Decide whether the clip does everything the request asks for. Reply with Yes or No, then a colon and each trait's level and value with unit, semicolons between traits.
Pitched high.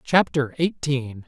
No: medium, 140 Hz